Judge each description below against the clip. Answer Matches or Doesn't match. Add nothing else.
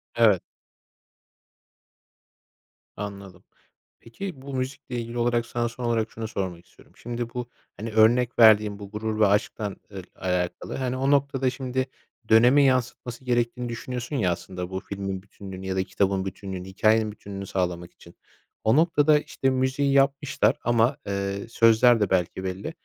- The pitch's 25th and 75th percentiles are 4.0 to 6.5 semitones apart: Matches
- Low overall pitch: Matches